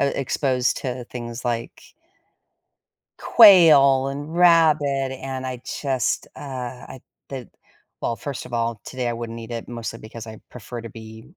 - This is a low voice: Yes, low, 125 Hz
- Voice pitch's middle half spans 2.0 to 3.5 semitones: Yes, average, 2.9 semitones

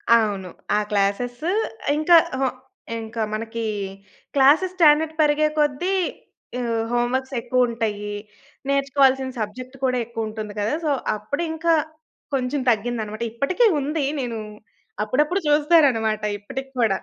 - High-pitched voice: Yes, very high, 255 Hz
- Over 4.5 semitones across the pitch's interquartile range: Yes, average, 4.9 semitones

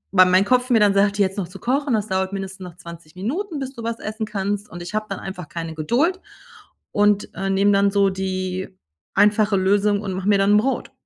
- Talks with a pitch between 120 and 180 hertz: No, high, 200 Hz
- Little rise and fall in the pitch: Yes, narrow, 2.2 semitones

